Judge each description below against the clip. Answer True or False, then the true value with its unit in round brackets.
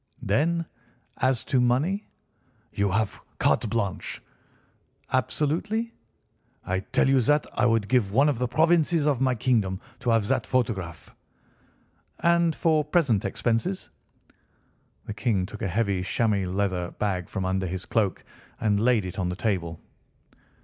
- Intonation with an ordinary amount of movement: False (6.2 semitones)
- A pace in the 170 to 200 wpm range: False (145 wpm)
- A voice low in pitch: True (115 Hz)